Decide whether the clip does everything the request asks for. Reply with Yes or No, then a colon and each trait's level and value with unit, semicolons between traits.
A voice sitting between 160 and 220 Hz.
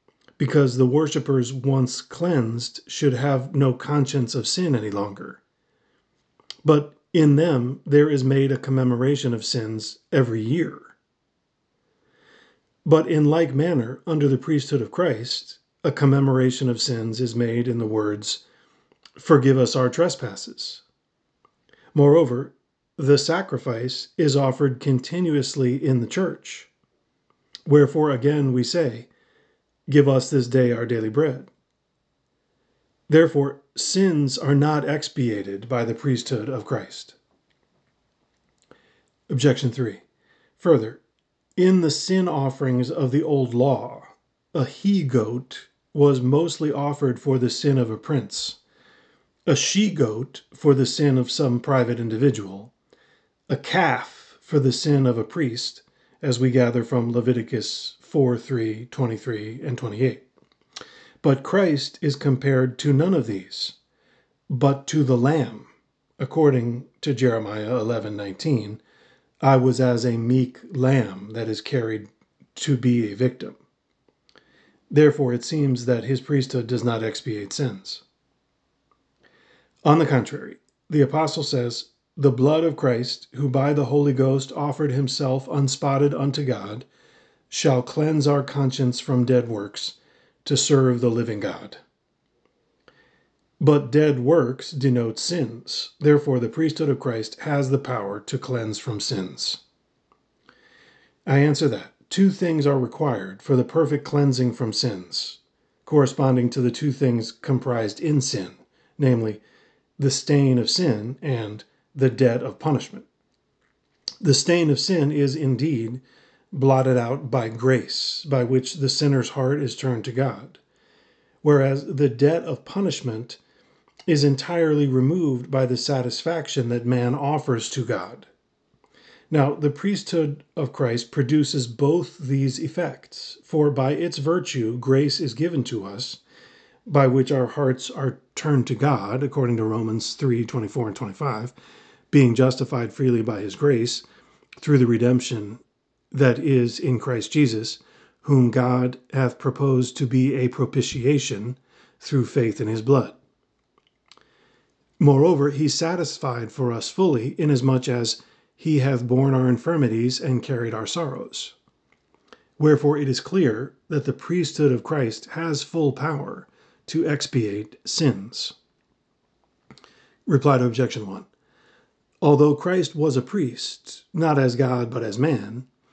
No: low, 135 Hz